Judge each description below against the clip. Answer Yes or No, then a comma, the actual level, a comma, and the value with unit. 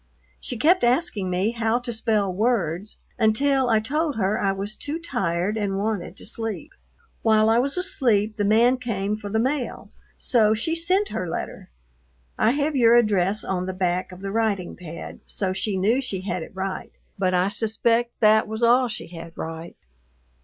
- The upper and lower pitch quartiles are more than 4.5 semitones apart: No, average, 4.0 semitones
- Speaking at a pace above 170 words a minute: Yes, average, 180 wpm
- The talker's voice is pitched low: No, high, 215 Hz